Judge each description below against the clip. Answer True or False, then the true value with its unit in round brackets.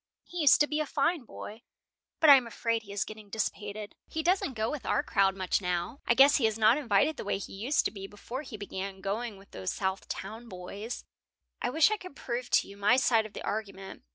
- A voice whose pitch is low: False (220 Hz)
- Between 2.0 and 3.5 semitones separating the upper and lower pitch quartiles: False (5.3 semitones)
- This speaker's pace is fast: True (240 wpm)